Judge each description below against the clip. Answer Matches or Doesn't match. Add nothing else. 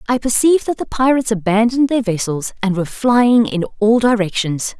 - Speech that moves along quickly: Doesn't match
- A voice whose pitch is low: Doesn't match